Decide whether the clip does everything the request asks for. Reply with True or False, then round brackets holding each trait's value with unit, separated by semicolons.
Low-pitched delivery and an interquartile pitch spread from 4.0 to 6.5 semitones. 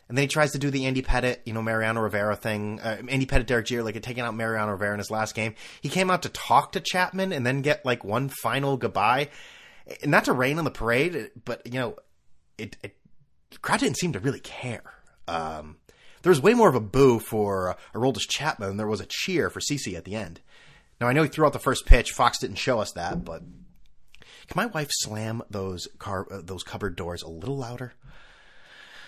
True (120 Hz; 4.6 semitones)